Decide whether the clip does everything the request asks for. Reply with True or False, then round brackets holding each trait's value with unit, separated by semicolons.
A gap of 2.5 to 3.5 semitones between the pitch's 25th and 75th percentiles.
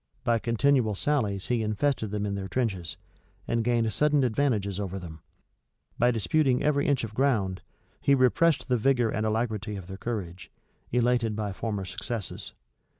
False (4.0 semitones)